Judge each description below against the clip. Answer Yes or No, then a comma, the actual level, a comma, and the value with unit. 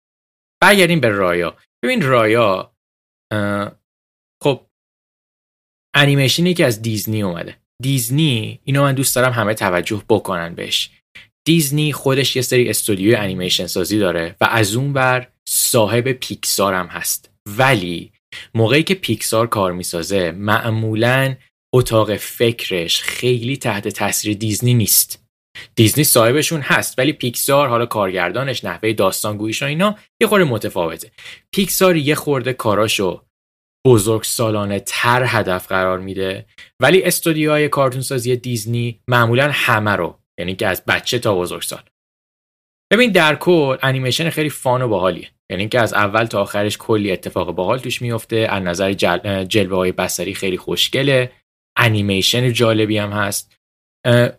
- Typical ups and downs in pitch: Yes, average, 4.3 semitones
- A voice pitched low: Yes, low, 115 Hz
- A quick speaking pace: No, average, 130 wpm